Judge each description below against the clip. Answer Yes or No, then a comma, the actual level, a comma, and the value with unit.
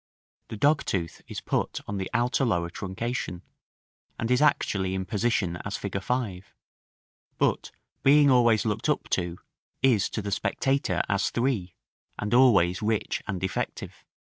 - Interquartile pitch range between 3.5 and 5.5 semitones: Yes, average, 4.6 semitones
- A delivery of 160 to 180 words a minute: No, average, 145 wpm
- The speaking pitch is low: Yes, low, 105 Hz